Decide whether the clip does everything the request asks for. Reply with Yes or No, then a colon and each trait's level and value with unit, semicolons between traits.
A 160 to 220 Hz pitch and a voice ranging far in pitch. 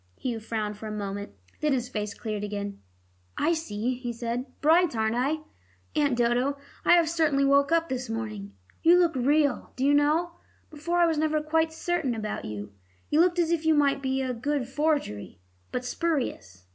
No: very high, 270 Hz; wide, 5.8 semitones